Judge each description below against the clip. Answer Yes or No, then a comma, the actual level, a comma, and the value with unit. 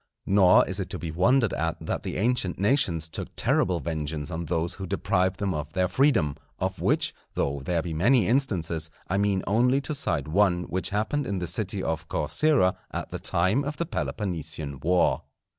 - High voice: No, very low, 90 Hz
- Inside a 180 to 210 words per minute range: Yes, average, 190 wpm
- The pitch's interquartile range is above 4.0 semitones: Yes, average, 4.5 semitones